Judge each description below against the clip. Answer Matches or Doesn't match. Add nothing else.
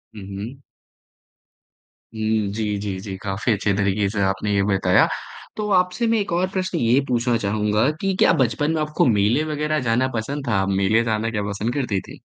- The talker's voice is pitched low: Matches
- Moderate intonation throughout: Doesn't match